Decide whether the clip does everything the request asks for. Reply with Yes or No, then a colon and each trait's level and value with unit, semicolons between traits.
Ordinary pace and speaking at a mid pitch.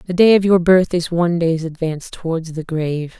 No: fast, 225 wpm; medium, 170 Hz